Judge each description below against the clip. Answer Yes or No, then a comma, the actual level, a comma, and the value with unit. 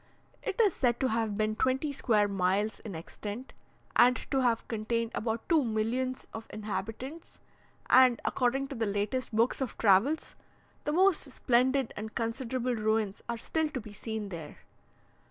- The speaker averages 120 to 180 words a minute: Yes, average, 155 wpm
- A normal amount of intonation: Yes, average, 3.3 semitones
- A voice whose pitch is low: No, high, 230 Hz